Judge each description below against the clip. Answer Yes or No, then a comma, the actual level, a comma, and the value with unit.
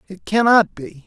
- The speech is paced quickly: No, average, 170 wpm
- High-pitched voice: Yes, high, 200 Hz